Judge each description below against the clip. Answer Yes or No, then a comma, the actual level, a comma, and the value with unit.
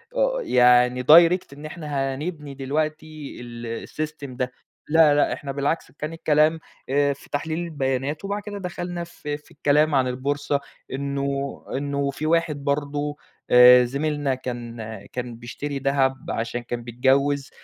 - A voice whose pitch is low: No, medium, 145 Hz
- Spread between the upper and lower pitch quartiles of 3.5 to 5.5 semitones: No, average, 2.7 semitones